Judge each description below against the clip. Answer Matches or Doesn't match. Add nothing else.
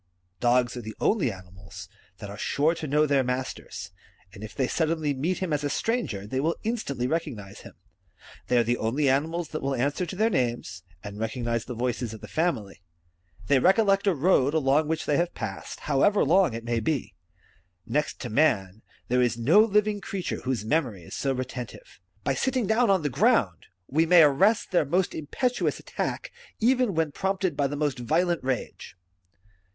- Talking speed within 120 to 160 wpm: Doesn't match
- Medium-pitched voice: Matches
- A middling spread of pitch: Doesn't match